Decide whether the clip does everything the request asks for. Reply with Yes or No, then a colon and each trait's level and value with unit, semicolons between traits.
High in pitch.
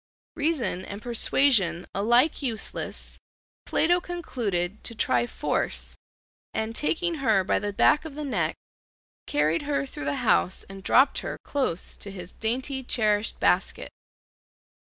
Yes: high, 225 Hz